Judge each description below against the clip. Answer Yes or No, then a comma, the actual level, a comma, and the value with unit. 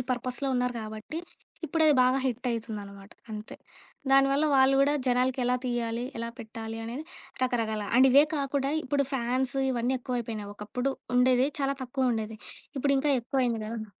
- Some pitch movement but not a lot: Yes, average, 3.0 semitones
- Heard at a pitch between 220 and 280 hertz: Yes, very high, 250 Hz